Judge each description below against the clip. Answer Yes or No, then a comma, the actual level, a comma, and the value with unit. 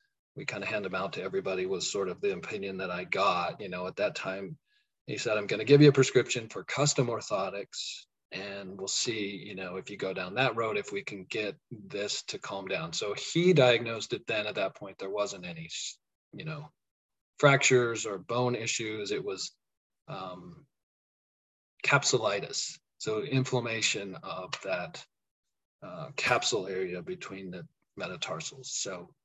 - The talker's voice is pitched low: Yes, low, 130 Hz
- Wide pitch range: Yes, wide, 7.3 semitones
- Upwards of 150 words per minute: Yes, average, 170 wpm